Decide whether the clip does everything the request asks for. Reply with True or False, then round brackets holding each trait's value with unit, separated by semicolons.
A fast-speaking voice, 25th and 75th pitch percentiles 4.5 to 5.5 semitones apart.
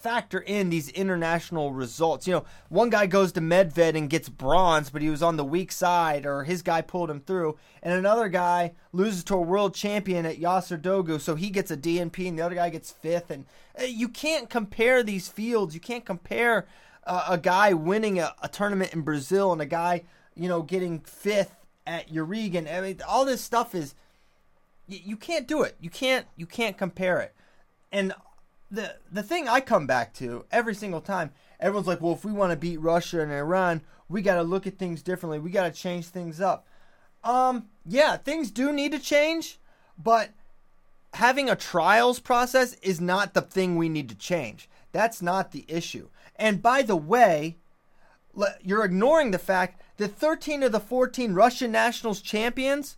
False (190 wpm; 4.8 semitones)